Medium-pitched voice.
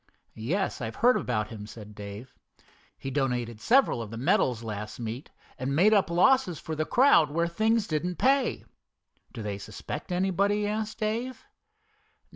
Yes: medium, 155 Hz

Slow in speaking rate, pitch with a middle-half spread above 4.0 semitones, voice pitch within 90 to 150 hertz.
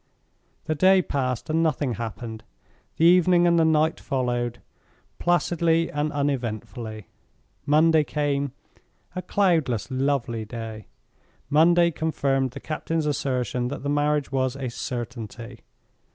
Yes: slow, 120 wpm; average, 4.7 semitones; medium, 140 Hz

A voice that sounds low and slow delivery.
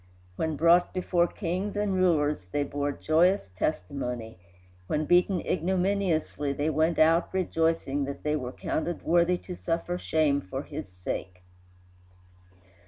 No: medium, 160 Hz; slow, 130 wpm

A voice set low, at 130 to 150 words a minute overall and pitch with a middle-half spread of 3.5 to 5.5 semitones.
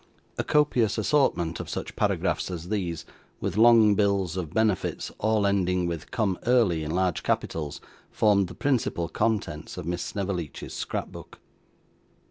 Yes: very low, 95 Hz; average, 140 wpm; average, 4.0 semitones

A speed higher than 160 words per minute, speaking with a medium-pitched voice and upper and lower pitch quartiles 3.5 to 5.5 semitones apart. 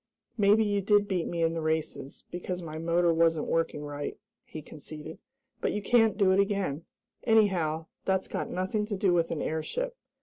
Yes: average, 180 wpm; medium, 175 Hz; average, 4.2 semitones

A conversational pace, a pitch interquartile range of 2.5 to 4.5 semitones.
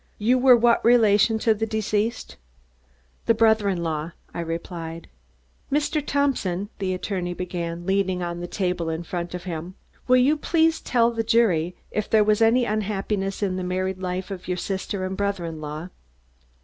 Yes: average, 175 wpm; average, 4.2 semitones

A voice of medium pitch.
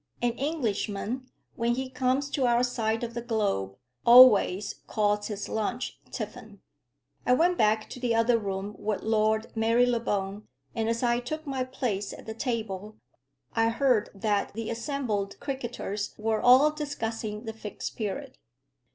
No: high, 230 Hz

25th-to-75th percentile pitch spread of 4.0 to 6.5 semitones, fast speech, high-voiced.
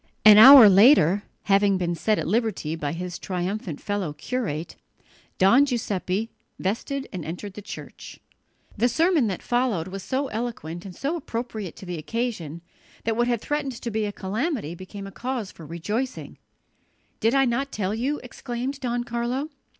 No: average, 5.0 semitones; average, 165 wpm; high, 215 Hz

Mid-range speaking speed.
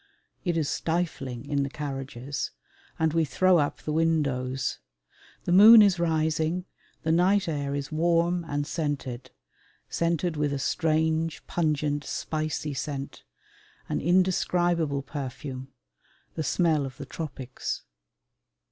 No: slow, 120 wpm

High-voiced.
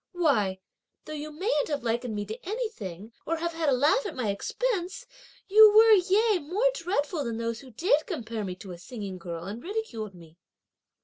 Yes: very high, 285 Hz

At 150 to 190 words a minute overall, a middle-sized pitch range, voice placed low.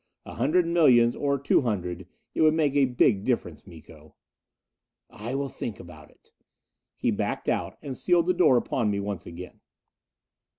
No: average, 165 wpm; wide, 6.7 semitones; low, 120 Hz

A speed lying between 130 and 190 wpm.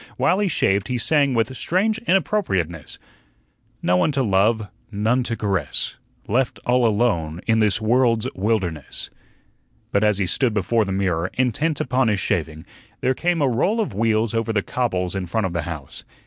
Yes: average, 175 wpm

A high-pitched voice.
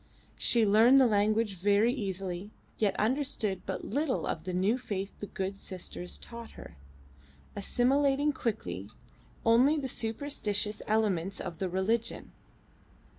Yes: high, 215 Hz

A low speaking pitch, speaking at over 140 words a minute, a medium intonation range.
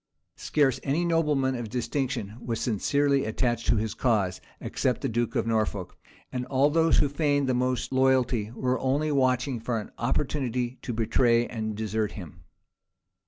Yes: low, 125 Hz; average, 160 wpm; average, 3.4 semitones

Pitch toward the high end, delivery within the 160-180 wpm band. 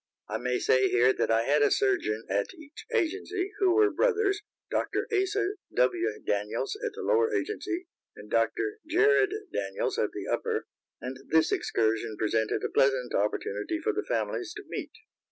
Yes: very high, 320 Hz; average, 165 wpm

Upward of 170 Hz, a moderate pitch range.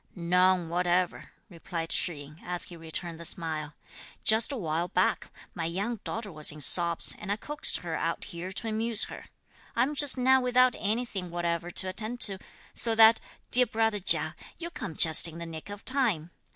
Yes: medium, 185 Hz; average, 5.0 semitones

